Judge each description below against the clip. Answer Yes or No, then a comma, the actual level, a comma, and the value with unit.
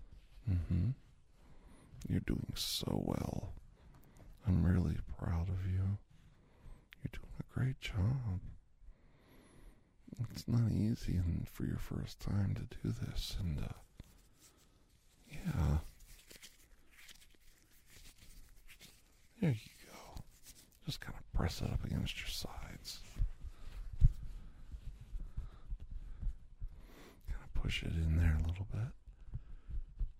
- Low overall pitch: Yes, very low, 95 Hz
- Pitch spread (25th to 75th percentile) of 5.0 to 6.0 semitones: Yes, wide, 5.5 semitones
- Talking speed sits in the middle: No, slow, 95 wpm